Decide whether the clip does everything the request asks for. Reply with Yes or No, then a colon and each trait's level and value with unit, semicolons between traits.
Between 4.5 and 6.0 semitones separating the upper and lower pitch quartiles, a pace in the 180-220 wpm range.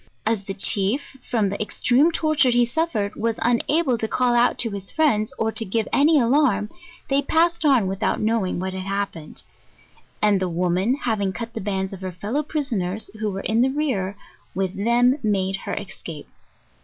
Yes: average, 4.9 semitones; average, 190 wpm